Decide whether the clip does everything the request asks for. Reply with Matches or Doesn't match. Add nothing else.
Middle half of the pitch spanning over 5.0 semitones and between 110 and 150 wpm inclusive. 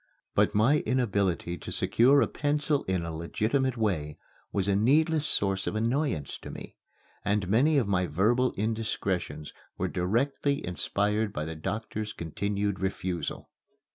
Matches